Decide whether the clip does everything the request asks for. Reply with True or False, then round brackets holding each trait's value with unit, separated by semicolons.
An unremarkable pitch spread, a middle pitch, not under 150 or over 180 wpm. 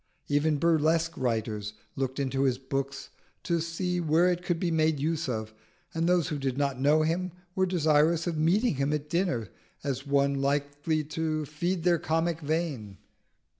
True (3.3 semitones; 155 Hz; 170 wpm)